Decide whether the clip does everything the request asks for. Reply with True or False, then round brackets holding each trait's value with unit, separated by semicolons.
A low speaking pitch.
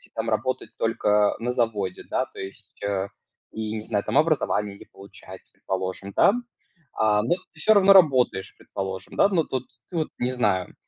True (110 Hz)